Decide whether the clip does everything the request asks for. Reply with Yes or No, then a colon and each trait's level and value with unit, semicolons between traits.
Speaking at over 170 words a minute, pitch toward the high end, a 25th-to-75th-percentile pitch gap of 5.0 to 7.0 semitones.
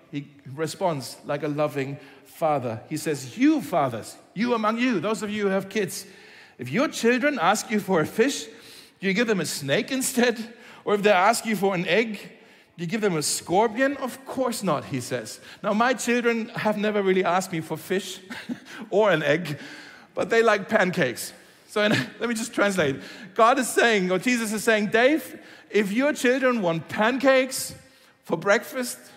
Yes: average, 185 wpm; high, 210 Hz; wide, 5.4 semitones